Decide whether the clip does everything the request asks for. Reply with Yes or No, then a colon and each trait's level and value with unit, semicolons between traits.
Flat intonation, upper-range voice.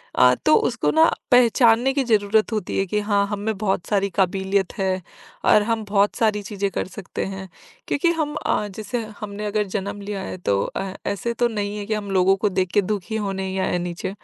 Yes: narrow, 2.3 semitones; high, 205 Hz